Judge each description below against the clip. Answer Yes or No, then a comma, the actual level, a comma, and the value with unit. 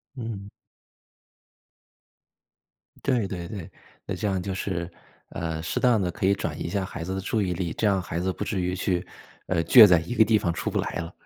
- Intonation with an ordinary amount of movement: Yes, average, 3.1 semitones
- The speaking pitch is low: Yes, very low, 95 Hz